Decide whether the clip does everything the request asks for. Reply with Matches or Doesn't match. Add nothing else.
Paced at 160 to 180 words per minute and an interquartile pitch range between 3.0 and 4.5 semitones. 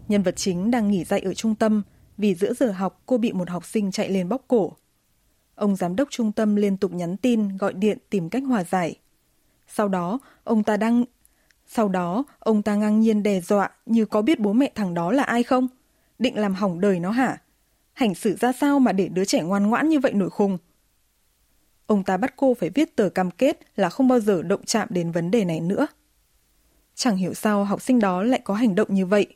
Doesn't match